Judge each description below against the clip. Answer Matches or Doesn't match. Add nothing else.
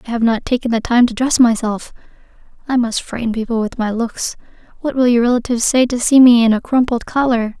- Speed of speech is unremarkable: Doesn't match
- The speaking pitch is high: Matches